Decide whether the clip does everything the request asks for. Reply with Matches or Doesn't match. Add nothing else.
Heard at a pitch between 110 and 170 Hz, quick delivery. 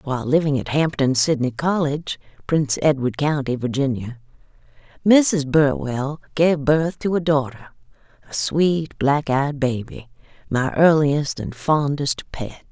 Doesn't match